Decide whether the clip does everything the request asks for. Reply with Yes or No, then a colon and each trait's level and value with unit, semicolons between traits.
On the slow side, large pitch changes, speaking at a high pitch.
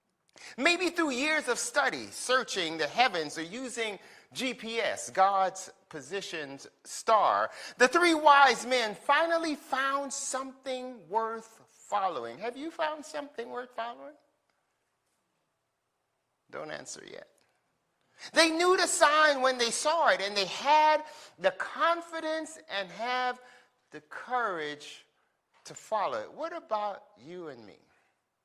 Yes: slow, 120 wpm; wide, 5.9 semitones; very high, 255 Hz